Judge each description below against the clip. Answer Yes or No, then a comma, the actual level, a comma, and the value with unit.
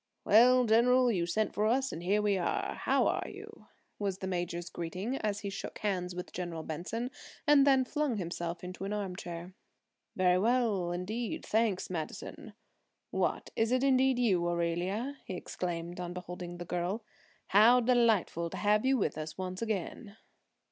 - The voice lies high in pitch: Yes, high, 195 Hz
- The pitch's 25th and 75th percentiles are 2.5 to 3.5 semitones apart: No, average, 4.9 semitones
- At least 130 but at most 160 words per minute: No, average, 170 wpm